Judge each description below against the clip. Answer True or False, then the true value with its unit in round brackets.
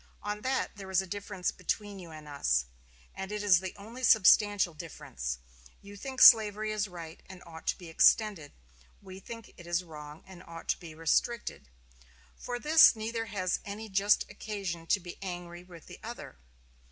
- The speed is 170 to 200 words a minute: True (175 wpm)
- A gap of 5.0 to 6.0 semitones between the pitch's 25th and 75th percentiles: False (3.7 semitones)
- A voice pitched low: False (190 Hz)